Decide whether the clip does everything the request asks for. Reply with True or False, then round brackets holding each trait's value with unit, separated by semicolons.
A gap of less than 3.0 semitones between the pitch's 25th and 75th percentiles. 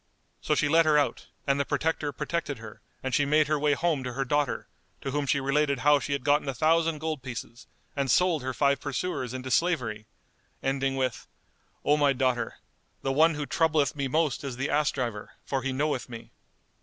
True (2.4 semitones)